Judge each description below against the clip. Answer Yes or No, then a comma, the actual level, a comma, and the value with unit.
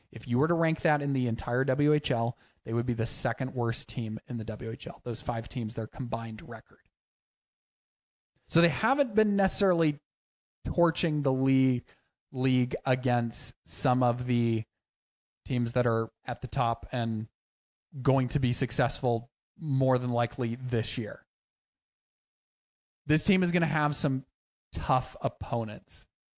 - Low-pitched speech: Yes, low, 125 Hz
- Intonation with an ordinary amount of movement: Yes, average, 3.9 semitones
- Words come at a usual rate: Yes, average, 145 wpm